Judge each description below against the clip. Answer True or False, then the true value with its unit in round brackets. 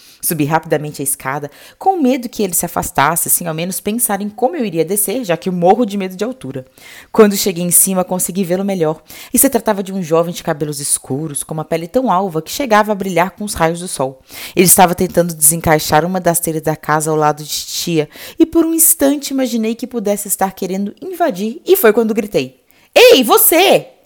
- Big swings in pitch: True (5.9 semitones)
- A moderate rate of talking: False (215 wpm)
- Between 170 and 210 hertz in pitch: True (185 Hz)